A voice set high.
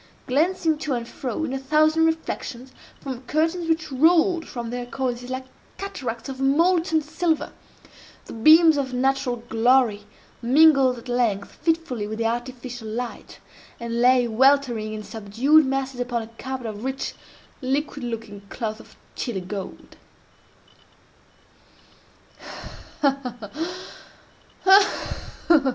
Yes: very high, 255 Hz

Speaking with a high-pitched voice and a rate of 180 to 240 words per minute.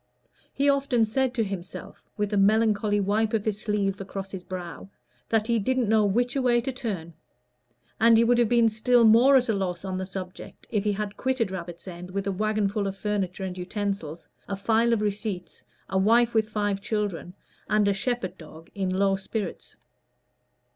Yes: high, 210 Hz; average, 190 wpm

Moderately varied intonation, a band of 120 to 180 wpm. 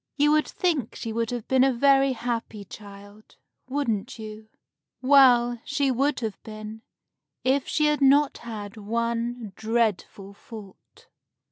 Yes: average, 3.9 semitones; average, 140 wpm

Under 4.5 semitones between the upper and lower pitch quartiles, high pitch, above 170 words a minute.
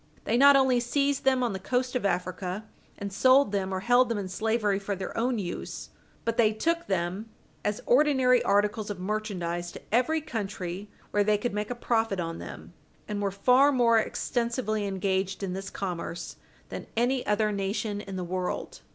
Yes: average, 4.0 semitones; high, 210 Hz; average, 185 wpm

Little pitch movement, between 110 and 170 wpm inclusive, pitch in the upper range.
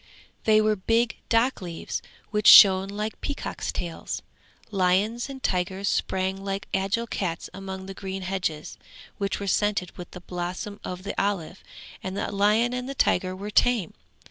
Yes: narrow, 2.3 semitones; average, 160 wpm; high, 195 Hz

